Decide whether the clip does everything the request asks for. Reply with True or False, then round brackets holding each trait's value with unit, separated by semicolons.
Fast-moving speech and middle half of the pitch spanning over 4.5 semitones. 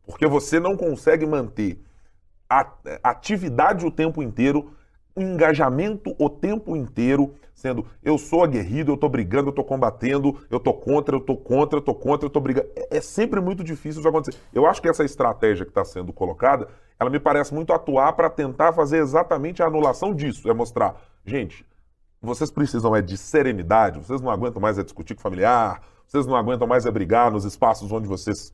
True (190 wpm; 5.1 semitones)